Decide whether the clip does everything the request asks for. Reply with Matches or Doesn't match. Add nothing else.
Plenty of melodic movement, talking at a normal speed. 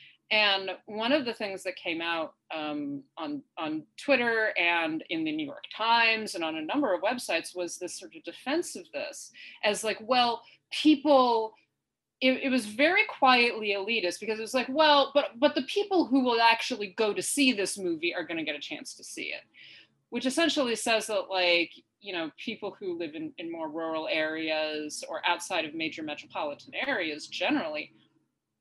Matches